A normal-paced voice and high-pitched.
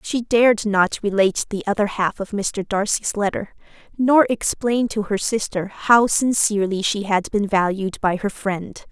Yes: average, 170 wpm; high, 205 Hz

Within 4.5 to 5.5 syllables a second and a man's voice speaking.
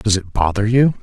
Yes: 5.1 syllables/s; male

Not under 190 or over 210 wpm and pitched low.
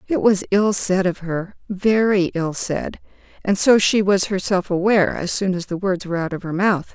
No: fast, 205 wpm; high, 190 Hz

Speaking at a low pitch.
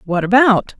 No: high, 220 Hz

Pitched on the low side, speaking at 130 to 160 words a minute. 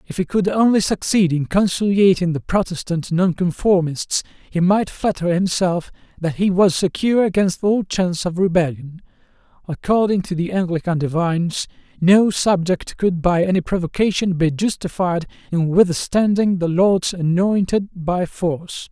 No: medium, 180 Hz; slow, 135 wpm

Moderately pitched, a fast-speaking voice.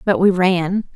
No: medium, 180 Hz; average, 190 wpm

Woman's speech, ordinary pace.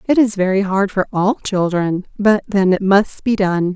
No: female; fast, 210 wpm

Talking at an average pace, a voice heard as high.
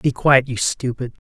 No: average, 190 wpm; low, 130 Hz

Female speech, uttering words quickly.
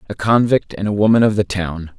No: male; fast, 240 wpm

